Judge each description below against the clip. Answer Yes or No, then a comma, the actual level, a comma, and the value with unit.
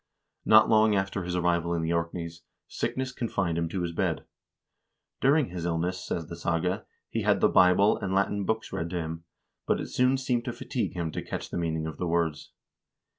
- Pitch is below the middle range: Yes, very low, 90 Hz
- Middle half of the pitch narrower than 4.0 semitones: Yes, average, 3.4 semitones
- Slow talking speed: No, average, 200 wpm